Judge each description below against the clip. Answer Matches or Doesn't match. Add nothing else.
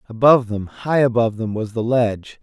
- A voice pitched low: Matches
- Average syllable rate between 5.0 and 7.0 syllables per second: Matches